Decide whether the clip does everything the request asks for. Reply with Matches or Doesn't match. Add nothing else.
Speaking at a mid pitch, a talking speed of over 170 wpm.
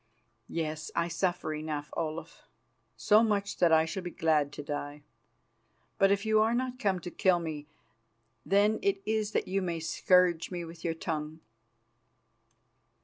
Doesn't match